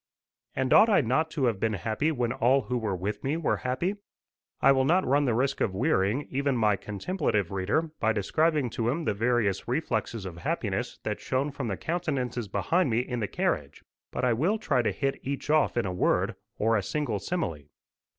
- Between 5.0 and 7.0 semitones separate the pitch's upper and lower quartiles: Yes, wide, 5.5 semitones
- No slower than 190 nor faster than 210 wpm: Yes, fast, 205 wpm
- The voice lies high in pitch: No, low, 125 Hz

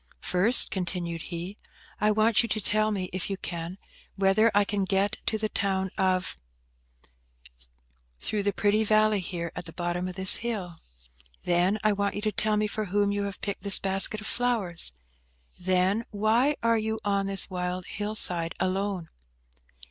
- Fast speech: No, average, 175 wpm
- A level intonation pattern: No, average, 3.0 semitones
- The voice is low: No, high, 195 Hz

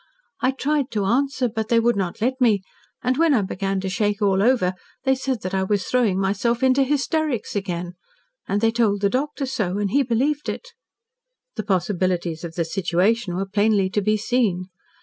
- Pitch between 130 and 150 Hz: No, high, 215 Hz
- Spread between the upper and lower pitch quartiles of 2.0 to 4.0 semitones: No, average, 4.9 semitones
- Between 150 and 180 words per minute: No, average, 190 wpm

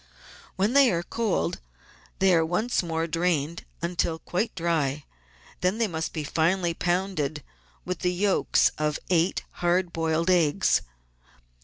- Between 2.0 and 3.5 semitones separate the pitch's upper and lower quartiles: Yes, narrow, 2.4 semitones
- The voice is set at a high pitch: No, medium, 170 Hz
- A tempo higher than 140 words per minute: No, slow, 135 wpm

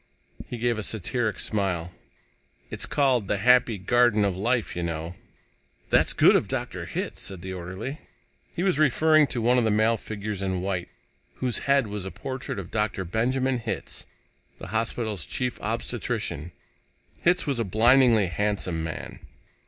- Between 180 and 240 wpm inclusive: No, average, 160 wpm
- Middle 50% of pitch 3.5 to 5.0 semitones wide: Yes, average, 4.6 semitones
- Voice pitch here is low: Yes, low, 110 Hz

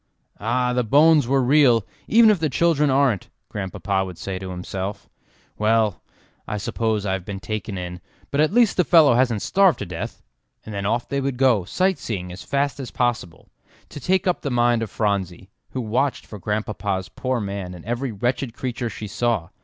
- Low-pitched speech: Yes, low, 115 Hz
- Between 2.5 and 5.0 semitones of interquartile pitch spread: No, wide, 5.6 semitones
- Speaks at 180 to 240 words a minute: Yes, average, 190 wpm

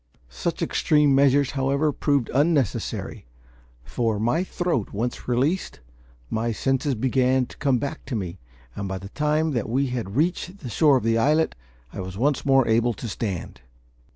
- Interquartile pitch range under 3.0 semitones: No, average, 4.3 semitones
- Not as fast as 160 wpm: No, average, 165 wpm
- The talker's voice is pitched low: Yes, low, 130 Hz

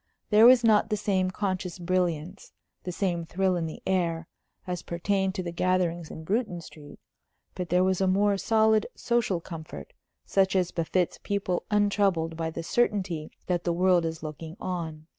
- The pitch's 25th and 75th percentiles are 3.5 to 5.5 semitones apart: No, average, 2.9 semitones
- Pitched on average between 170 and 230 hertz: Yes, medium, 185 Hz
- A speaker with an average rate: Yes, average, 170 wpm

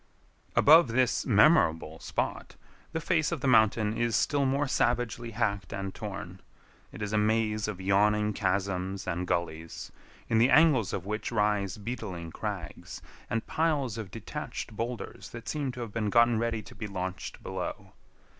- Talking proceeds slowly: No, average, 160 wpm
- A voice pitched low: Yes, low, 110 Hz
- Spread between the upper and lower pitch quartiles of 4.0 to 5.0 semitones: No, average, 3.6 semitones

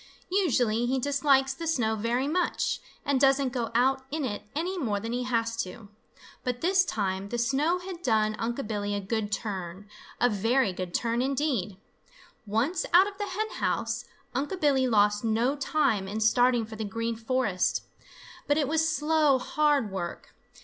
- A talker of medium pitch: No, high, 245 Hz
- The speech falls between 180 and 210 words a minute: No, average, 170 wpm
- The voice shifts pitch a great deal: No, average, 4.9 semitones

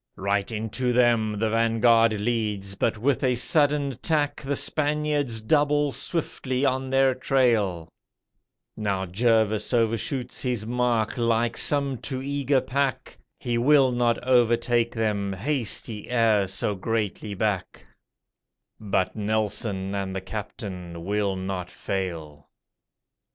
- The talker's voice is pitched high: No, low, 115 Hz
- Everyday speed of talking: No, slow, 120 wpm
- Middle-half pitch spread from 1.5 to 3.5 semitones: No, average, 4.2 semitones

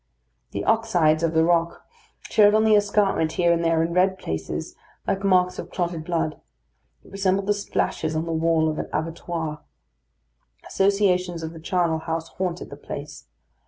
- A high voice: No, medium, 170 Hz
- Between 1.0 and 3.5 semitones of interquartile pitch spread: Yes, average, 3.0 semitones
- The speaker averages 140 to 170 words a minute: Yes, average, 165 wpm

